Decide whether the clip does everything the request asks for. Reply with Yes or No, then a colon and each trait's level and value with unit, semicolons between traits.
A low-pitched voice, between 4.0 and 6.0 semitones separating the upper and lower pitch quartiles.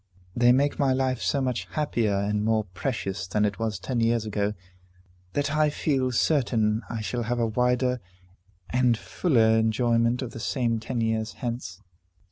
No: low, 115 Hz; average, 2.8 semitones